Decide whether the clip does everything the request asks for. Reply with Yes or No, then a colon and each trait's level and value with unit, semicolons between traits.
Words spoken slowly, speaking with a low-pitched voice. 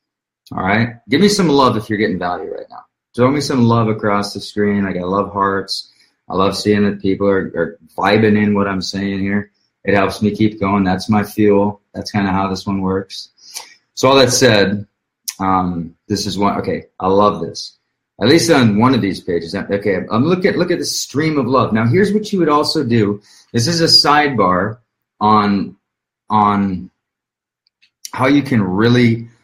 No: average, 200 wpm; low, 105 Hz